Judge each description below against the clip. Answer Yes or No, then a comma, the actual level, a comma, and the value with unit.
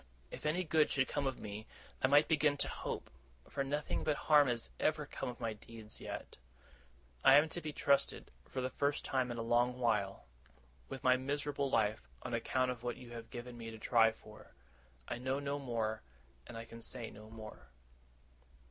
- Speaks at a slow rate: No, average, 195 wpm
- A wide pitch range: No, average, 3.8 semitones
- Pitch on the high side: No, low, 125 Hz